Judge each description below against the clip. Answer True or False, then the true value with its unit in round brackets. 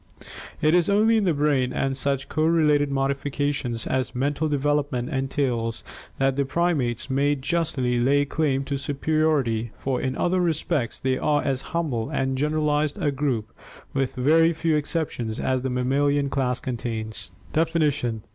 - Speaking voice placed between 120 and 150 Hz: True (140 Hz)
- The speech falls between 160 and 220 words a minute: False (145 wpm)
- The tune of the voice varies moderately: True (3.0 semitones)